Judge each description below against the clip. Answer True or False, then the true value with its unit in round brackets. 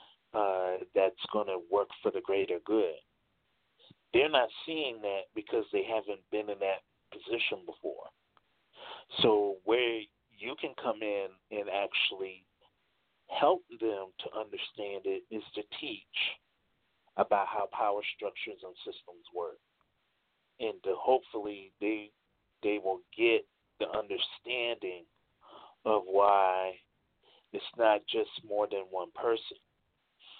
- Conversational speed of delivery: False (120 wpm)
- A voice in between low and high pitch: False (115 Hz)